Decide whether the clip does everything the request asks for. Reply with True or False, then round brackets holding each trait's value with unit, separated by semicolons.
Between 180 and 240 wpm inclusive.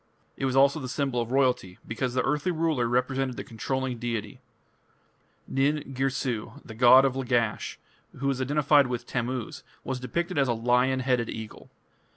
False (165 wpm)